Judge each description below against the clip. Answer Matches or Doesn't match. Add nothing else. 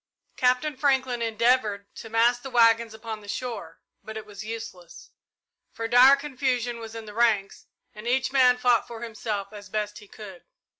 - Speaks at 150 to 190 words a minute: Matches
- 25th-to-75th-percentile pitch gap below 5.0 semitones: Matches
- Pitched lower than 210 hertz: Doesn't match